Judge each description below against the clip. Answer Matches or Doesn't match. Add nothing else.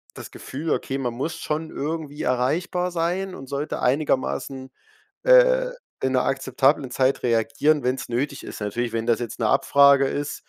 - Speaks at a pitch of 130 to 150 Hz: Matches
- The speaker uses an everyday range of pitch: Matches